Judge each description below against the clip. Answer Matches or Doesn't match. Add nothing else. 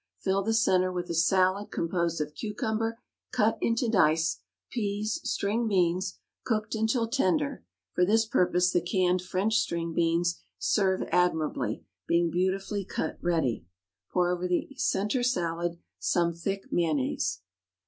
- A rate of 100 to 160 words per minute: Matches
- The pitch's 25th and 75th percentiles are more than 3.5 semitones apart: Matches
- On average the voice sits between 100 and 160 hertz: Doesn't match